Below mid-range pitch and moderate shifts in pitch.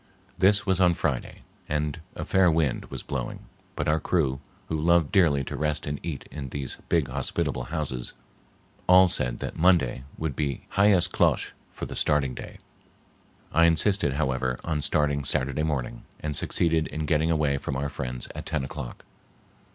Yes: very low, 75 Hz; average, 3.5 semitones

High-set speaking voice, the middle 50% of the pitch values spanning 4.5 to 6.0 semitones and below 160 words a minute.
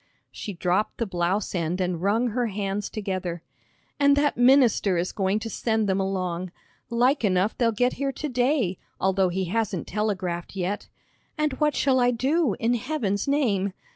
No: high, 210 Hz; average, 4.8 semitones; average, 170 wpm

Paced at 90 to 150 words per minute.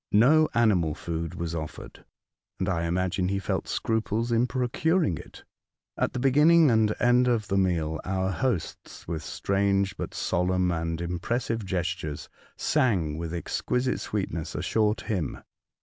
Yes: average, 145 wpm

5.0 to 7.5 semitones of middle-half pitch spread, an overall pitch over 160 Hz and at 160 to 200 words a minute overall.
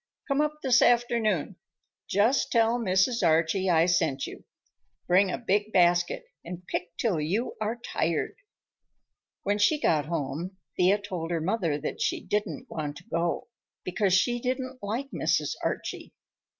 No: wide, 5.4 semitones; high, 190 Hz; average, 150 wpm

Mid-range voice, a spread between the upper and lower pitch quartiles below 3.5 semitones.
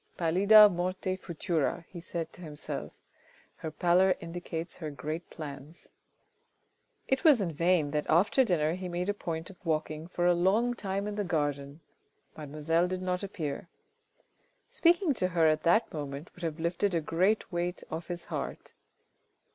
Yes: medium, 175 Hz; average, 3.0 semitones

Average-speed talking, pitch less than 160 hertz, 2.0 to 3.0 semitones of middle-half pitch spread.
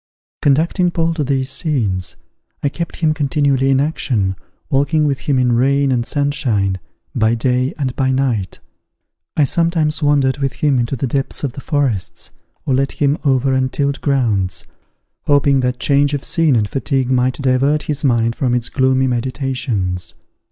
Yes: average, 160 wpm; low, 135 Hz; narrow, 2.5 semitones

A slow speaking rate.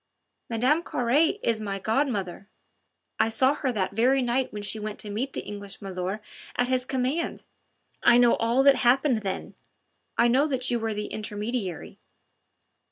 No: average, 165 wpm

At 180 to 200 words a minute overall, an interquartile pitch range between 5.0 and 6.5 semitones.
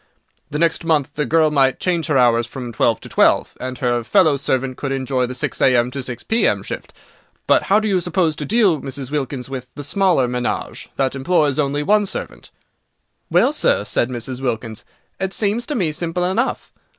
Yes: average, 195 wpm; average, 5.3 semitones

